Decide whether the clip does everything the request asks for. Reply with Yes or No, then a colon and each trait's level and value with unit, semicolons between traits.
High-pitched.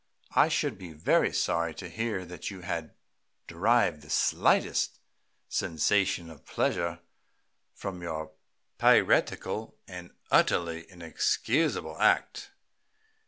No: very low, 85 Hz